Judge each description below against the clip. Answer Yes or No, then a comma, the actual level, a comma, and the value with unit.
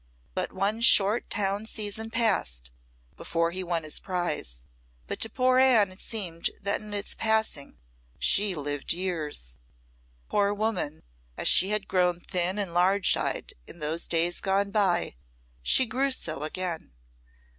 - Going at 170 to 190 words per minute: No, average, 145 wpm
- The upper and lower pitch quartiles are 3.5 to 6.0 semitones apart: Yes, average, 3.9 semitones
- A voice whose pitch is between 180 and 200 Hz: Yes, high, 190 Hz